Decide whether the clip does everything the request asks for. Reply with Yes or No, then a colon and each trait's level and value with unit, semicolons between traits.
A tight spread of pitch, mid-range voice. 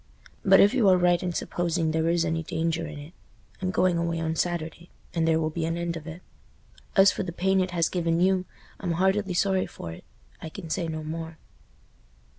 Yes: narrow, 2.2 semitones; medium, 170 Hz